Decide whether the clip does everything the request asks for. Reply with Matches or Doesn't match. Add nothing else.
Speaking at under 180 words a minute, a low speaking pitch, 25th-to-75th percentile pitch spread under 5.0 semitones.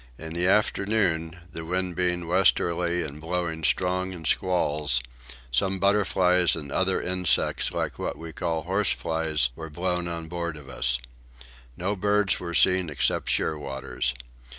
Matches